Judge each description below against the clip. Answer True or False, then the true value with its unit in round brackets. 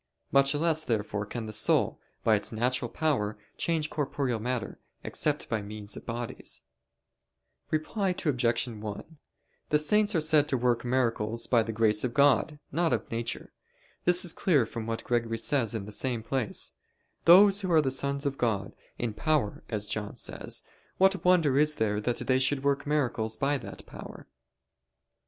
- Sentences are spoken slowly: False (165 wpm)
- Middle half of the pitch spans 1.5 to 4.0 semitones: False (5.1 semitones)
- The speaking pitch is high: False (130 Hz)